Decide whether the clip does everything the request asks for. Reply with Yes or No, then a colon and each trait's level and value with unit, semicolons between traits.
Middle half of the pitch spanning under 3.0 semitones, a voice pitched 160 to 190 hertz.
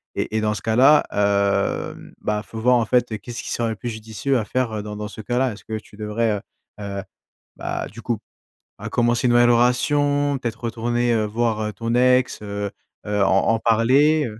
No: narrow, 2.5 semitones; low, 115 Hz